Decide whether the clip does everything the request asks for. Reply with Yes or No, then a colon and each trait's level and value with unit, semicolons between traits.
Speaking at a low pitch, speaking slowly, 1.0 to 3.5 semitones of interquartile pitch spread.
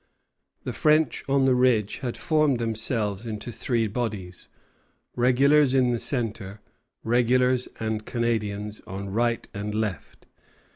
Yes: low, 115 Hz; slow, 125 wpm; average, 3.1 semitones